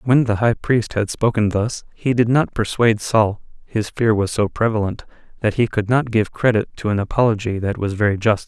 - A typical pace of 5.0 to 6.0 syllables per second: Yes, 5.2 syllables/s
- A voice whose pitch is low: Yes, low, 110 Hz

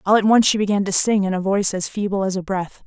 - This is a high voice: Yes, high, 195 Hz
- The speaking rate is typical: No, fast, 315 wpm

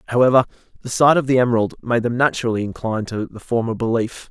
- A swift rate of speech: No, average, 195 wpm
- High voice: No, low, 120 Hz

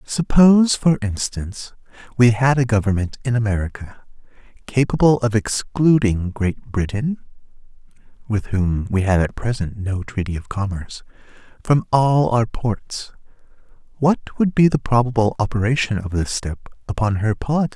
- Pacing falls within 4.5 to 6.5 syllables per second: No, 4.0 syllables/s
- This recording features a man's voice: Yes, male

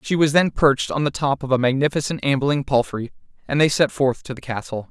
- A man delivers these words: Yes, male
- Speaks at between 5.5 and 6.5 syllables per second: Yes, 5.8 syllables/s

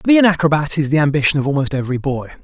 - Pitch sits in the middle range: Yes, medium, 150 Hz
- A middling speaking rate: No, fast, 270 wpm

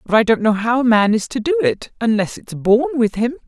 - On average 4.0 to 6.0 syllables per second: Yes, 5.3 syllables/s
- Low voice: No, high, 235 Hz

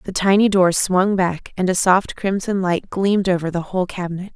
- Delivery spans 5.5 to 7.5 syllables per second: No, 5.3 syllables/s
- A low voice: No, medium, 185 Hz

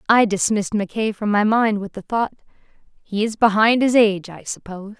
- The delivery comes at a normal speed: Yes, average, 190 wpm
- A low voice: No, high, 210 Hz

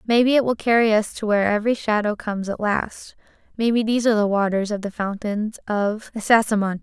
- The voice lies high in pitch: Yes, high, 215 Hz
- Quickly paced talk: No, average, 195 wpm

